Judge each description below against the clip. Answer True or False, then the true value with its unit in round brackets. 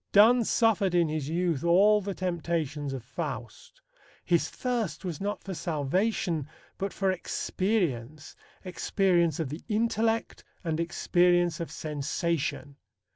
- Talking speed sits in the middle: False (125 wpm)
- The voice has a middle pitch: True (175 Hz)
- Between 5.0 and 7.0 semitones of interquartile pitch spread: False (4.4 semitones)